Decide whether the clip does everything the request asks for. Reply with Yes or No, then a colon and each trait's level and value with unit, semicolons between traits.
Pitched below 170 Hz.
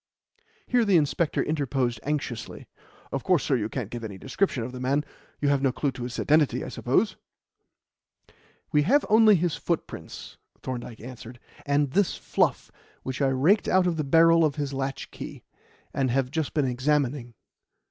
Yes: medium, 140 Hz